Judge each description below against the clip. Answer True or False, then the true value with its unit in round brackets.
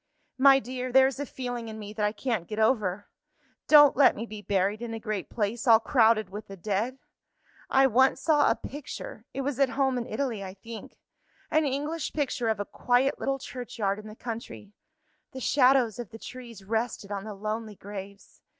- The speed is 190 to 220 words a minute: True (195 wpm)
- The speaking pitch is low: False (230 Hz)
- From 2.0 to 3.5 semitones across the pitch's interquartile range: False (3.9 semitones)